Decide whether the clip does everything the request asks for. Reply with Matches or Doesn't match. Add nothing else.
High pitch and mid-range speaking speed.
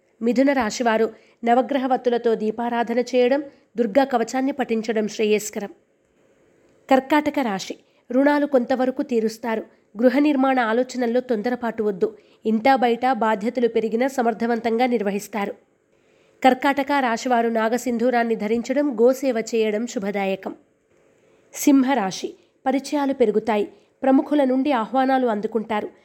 Matches